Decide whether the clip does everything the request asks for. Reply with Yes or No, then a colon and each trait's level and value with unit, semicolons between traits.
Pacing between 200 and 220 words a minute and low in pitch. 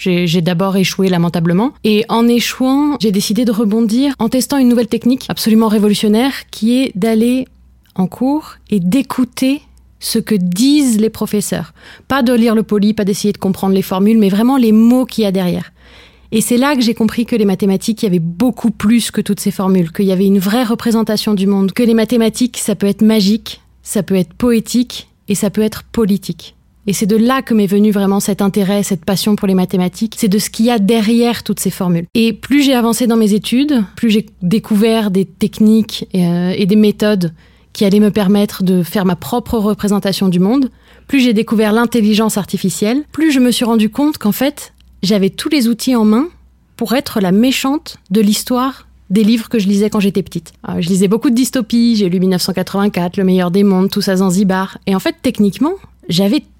No: average, 210 wpm; high, 215 Hz